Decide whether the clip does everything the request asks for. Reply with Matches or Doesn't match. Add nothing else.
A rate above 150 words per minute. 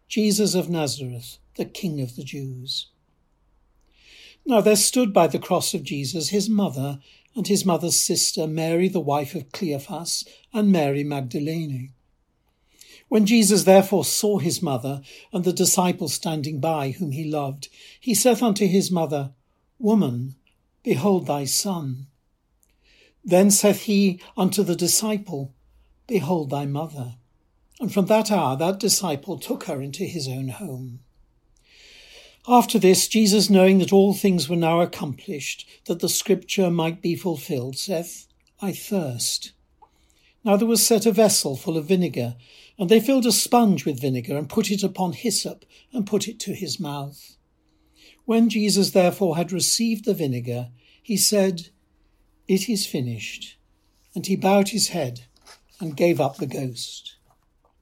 Doesn't match